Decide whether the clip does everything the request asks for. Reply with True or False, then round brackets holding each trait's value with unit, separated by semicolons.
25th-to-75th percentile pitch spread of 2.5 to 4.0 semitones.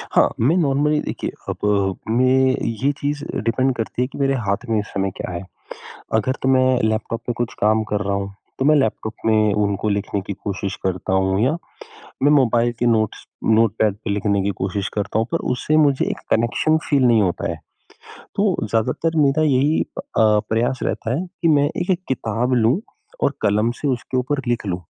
False (4.6 semitones)